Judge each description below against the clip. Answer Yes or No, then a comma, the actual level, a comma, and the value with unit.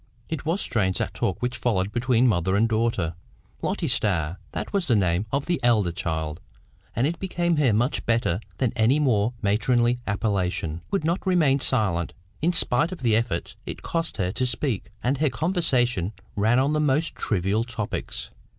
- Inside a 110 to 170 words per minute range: No, average, 180 wpm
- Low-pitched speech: Yes, low, 120 Hz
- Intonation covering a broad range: Yes, wide, 6.0 semitones